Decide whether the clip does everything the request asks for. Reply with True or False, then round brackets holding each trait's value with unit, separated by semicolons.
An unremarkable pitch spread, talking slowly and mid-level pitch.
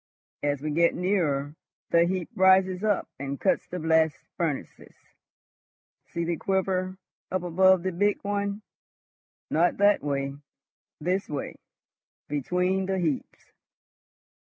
True (3.6 semitones; 120 wpm; 180 Hz)